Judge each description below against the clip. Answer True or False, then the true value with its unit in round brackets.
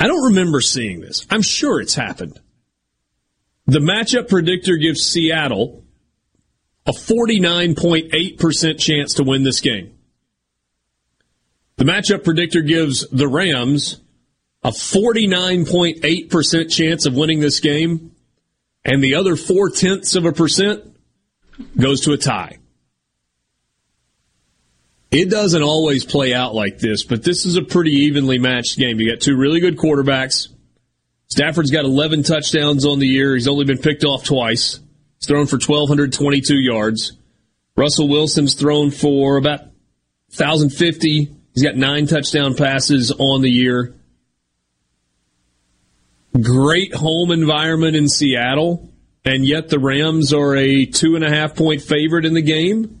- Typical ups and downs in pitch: True (4.2 semitones)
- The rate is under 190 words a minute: True (135 wpm)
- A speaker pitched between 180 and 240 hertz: False (145 Hz)